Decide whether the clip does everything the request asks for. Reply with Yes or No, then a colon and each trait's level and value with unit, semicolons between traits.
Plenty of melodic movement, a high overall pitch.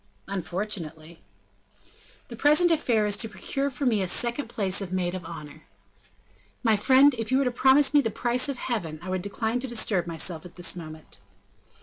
Yes: wide, 6.0 semitones; high, 210 Hz